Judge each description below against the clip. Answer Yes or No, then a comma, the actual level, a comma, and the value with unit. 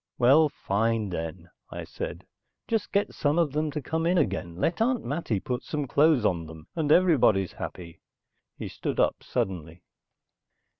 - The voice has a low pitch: Yes, low, 125 Hz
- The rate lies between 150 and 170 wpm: Yes, average, 160 wpm